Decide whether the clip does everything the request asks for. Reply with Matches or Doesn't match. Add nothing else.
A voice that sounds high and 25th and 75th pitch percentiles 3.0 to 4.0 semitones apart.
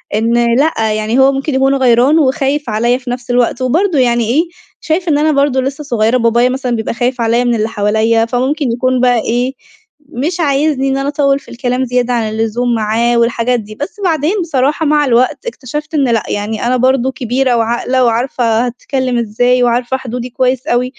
Doesn't match